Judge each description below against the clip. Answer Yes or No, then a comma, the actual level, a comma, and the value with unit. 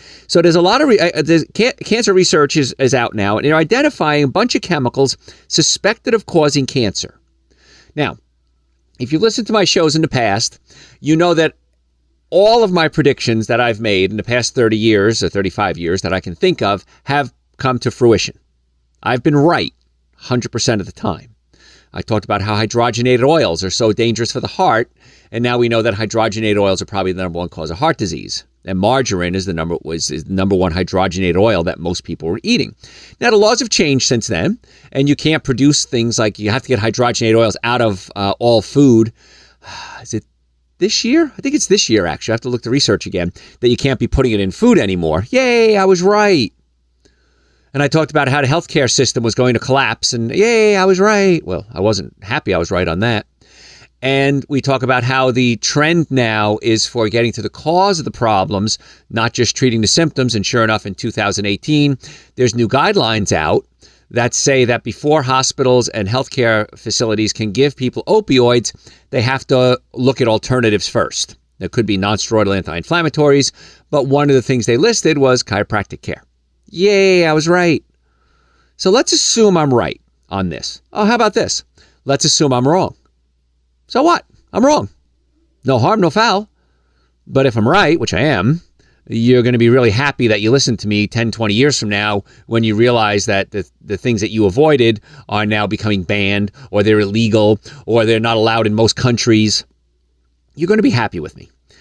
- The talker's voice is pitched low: Yes, low, 115 Hz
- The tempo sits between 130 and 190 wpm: No, average, 200 wpm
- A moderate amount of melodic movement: No, wide, 5.9 semitones